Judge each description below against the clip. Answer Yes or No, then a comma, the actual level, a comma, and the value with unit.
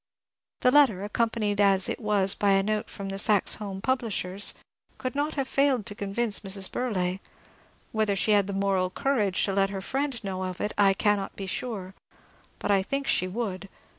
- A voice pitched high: Yes, high, 205 Hz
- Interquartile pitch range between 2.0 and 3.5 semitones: Yes, average, 3.1 semitones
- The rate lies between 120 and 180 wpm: No, average, 190 wpm